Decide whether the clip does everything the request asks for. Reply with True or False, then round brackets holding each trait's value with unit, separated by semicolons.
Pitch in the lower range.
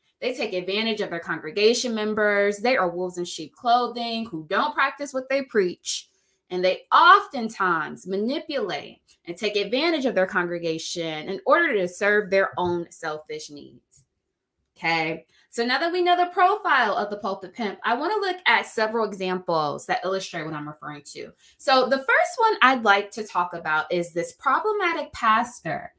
False (205 Hz)